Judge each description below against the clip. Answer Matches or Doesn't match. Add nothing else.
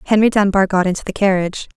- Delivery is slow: Doesn't match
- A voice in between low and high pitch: Doesn't match